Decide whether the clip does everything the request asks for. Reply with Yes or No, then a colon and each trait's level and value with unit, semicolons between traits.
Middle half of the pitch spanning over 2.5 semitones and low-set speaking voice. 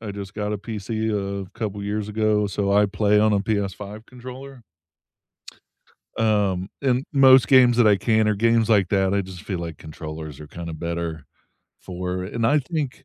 Yes: average, 2.9 semitones; low, 105 Hz